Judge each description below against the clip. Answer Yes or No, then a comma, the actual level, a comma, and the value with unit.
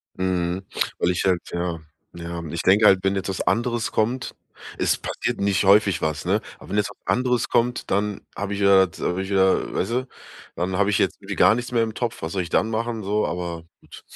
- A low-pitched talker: Yes, low, 100 Hz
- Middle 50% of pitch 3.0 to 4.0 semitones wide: Yes, average, 3.6 semitones